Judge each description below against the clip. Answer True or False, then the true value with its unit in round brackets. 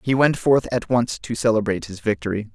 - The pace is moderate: False (210 wpm)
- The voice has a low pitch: True (115 Hz)